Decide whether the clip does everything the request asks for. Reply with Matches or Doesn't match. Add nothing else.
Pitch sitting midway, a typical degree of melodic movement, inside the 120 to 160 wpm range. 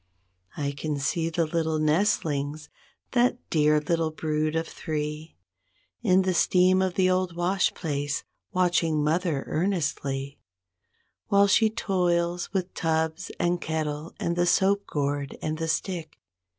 Matches